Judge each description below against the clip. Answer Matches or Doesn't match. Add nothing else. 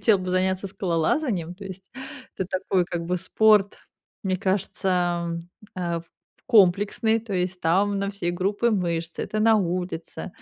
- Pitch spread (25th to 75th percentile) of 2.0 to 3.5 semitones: Matches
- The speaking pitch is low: Doesn't match